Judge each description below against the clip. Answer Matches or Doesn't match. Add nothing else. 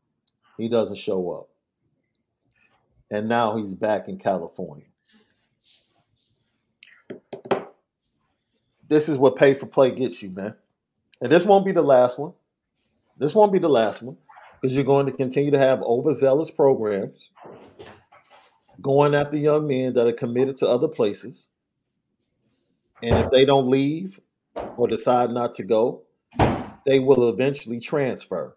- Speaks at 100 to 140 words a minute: Matches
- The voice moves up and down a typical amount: Matches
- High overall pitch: Doesn't match